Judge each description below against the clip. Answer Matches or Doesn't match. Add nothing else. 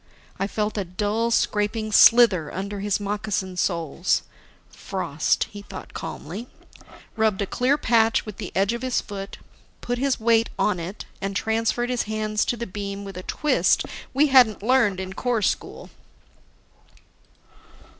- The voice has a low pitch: Doesn't match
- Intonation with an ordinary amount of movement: Matches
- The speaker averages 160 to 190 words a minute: Doesn't match